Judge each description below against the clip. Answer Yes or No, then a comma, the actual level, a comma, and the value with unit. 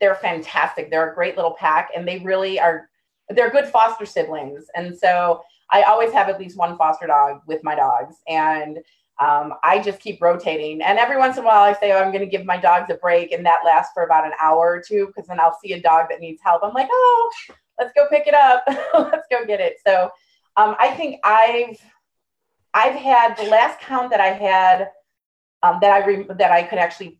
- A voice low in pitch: No, high, 190 Hz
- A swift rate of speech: Yes, fast, 225 wpm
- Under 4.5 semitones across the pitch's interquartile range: No, average, 5.0 semitones